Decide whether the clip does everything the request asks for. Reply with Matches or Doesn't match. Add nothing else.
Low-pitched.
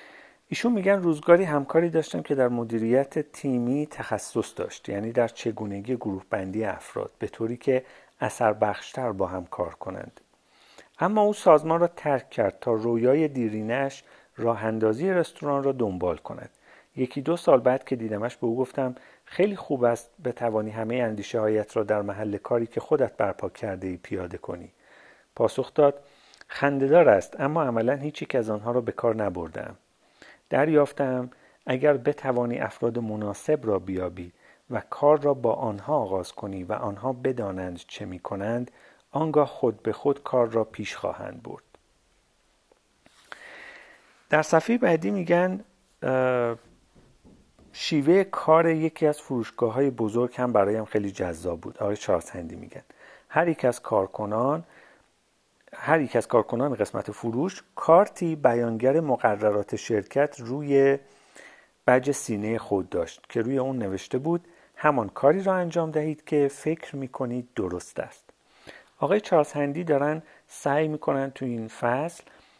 Matches